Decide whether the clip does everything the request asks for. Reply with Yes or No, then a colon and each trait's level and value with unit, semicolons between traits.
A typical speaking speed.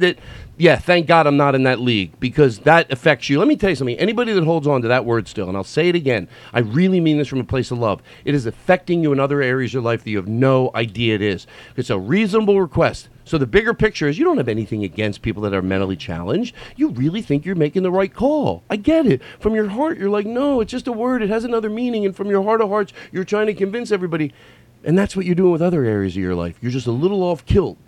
No: fast, 280 wpm